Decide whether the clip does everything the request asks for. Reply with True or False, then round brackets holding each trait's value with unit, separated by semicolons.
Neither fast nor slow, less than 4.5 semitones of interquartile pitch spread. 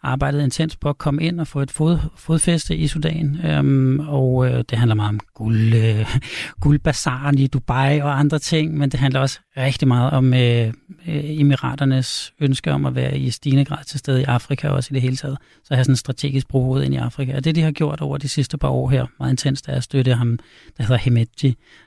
False (240 wpm; 2.4 semitones)